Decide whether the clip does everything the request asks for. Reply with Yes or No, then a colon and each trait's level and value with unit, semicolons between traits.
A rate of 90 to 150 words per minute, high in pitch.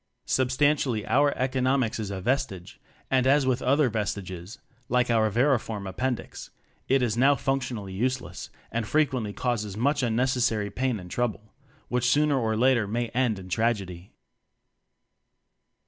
No: average, 145 wpm; low, 120 Hz